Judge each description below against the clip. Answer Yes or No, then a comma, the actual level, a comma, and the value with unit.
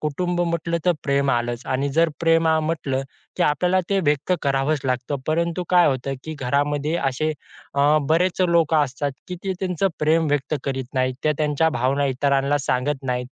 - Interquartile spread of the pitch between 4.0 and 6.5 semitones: No, average, 3.4 semitones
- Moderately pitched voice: Yes, medium, 150 Hz